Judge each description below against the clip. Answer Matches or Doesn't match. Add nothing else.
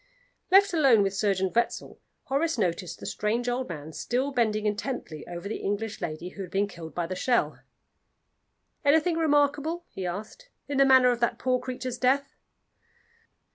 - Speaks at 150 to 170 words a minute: Matches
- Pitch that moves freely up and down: Matches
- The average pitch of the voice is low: Doesn't match